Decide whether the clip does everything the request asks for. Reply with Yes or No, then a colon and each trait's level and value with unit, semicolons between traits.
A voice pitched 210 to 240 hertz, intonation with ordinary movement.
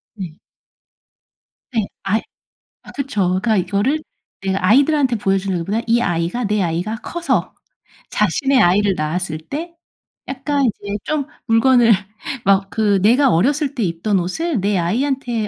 No: high, 215 Hz; wide, 5.7 semitones